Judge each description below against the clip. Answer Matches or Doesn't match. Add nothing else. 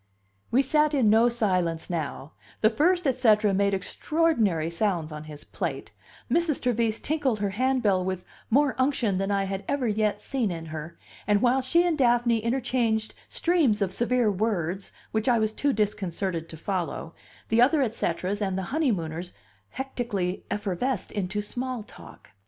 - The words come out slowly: Doesn't match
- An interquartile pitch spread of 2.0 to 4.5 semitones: Doesn't match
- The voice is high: Matches